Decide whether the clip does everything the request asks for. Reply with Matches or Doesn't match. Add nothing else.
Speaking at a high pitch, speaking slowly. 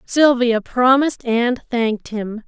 Matches